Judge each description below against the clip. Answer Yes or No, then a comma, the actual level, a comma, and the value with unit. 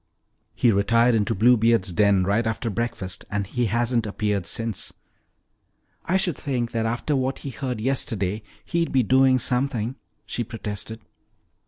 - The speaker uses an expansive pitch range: No, average, 3.3 semitones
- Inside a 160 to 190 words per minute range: No, average, 145 wpm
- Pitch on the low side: Yes, low, 115 Hz